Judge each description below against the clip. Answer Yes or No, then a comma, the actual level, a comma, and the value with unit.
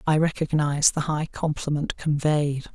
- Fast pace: No, slow, 130 wpm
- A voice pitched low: No, medium, 150 Hz